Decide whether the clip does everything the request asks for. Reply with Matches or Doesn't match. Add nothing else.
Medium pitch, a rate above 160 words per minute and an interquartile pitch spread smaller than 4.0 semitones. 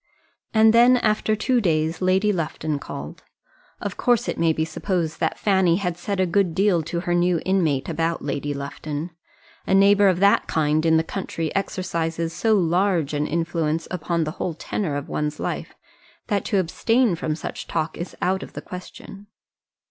Matches